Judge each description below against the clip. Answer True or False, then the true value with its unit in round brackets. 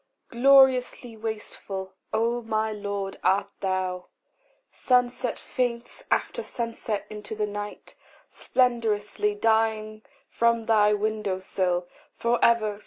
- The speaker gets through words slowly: True (105 wpm)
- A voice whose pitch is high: True (215 Hz)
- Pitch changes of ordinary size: False (2.3 semitones)